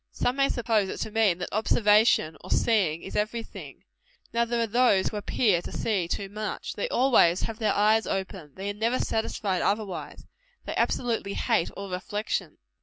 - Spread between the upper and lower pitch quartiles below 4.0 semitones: Yes, average, 2.9 semitones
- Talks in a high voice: Yes, high, 210 Hz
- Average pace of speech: Yes, average, 180 wpm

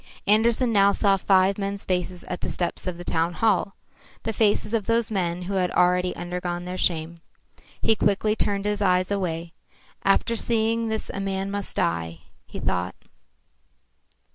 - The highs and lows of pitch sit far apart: No, average, 2.8 semitones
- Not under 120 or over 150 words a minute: No, average, 165 wpm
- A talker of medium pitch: No, high, 195 Hz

